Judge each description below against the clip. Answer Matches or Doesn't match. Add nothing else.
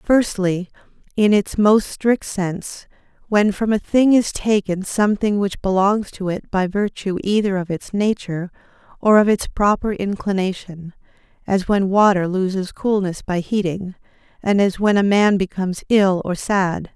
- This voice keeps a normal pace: Matches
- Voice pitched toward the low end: Doesn't match